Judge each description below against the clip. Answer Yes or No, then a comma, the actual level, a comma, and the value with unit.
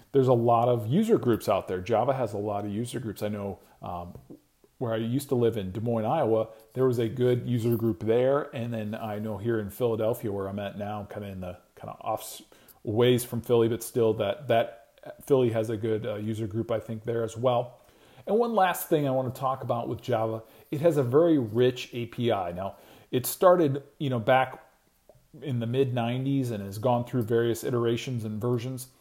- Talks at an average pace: No, fast, 220 wpm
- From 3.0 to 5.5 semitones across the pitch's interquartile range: No, narrow, 2.6 semitones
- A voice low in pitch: Yes, low, 120 Hz